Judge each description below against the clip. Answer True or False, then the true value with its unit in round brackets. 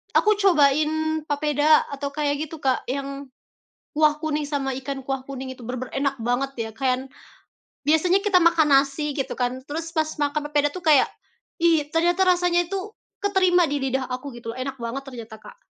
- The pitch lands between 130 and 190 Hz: False (290 Hz)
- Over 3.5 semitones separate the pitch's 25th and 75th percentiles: False (2.9 semitones)